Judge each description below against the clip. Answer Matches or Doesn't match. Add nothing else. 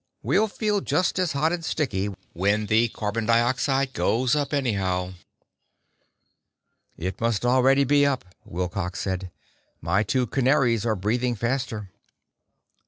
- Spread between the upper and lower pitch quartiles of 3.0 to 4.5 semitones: Doesn't match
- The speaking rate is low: Matches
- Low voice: Matches